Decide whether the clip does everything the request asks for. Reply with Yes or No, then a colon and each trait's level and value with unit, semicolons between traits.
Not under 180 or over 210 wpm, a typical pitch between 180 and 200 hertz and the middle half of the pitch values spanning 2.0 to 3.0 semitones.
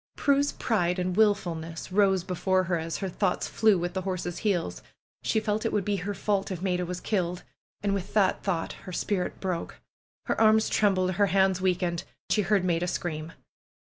Yes: average, 185 wpm; medium, 185 Hz; narrow, 2.5 semitones